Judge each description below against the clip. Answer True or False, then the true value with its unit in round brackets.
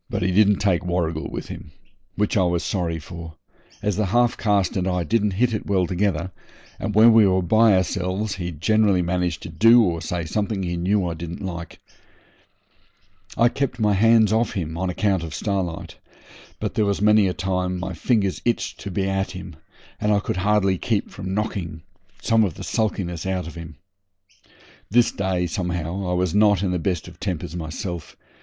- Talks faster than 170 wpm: True (190 wpm)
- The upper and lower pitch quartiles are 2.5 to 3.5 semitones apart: True (3.1 semitones)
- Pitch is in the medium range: False (95 Hz)